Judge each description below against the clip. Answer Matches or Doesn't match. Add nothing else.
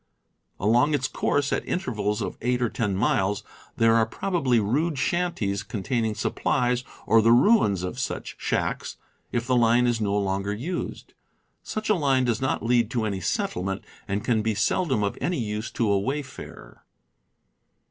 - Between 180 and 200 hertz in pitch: Doesn't match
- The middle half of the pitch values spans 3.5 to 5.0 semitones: Matches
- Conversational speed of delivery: Matches